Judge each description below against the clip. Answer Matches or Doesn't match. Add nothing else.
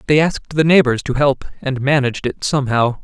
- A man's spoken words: Matches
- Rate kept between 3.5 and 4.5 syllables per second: Doesn't match